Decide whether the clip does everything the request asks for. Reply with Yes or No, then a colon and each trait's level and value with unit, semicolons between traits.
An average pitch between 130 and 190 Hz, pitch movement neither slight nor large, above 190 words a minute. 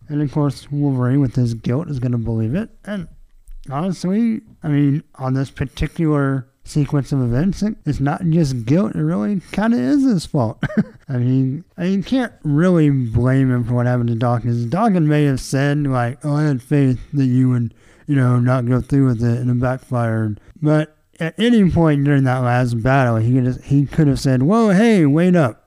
Yes: medium, 140 Hz; average, 4.5 semitones; fast, 205 wpm